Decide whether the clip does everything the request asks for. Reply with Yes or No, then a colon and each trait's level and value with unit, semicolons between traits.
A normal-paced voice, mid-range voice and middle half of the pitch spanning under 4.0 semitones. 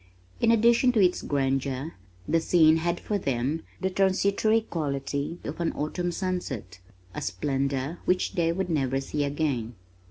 No: average, 150 wpm; medium, 160 Hz; average, 5.1 semitones